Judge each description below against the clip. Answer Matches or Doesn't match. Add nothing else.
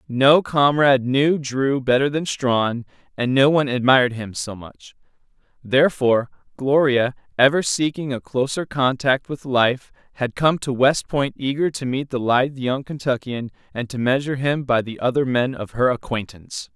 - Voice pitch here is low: Matches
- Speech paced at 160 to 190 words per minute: Matches